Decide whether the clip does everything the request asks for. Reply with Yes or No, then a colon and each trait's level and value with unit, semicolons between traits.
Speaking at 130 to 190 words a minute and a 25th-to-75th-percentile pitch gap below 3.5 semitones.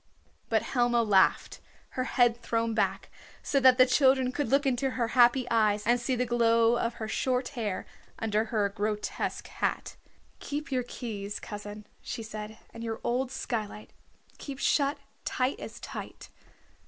Yes: average, 155 wpm; average, 2.8 semitones